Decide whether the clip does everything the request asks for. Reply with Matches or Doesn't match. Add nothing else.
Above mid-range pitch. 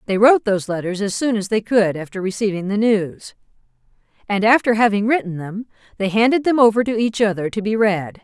Matches